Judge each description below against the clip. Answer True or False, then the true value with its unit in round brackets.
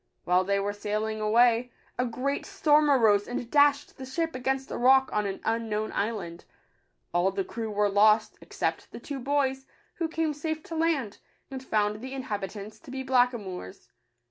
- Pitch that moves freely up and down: False (4.6 semitones)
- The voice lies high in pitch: True (245 Hz)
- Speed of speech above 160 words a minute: True (170 wpm)